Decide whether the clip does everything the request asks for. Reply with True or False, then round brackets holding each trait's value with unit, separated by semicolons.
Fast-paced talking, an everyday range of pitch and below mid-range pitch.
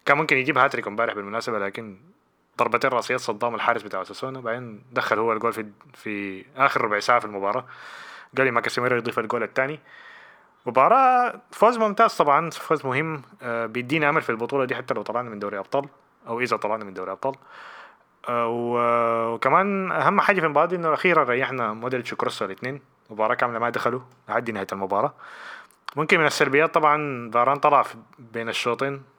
True (170 wpm; 4.1 semitones; 125 Hz)